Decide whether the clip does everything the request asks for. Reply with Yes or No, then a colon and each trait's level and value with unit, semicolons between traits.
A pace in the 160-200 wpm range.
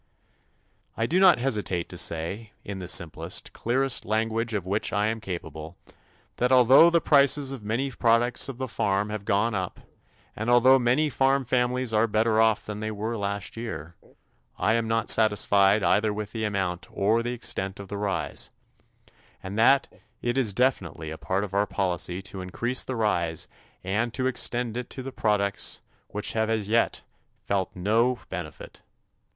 Yes: average, 170 wpm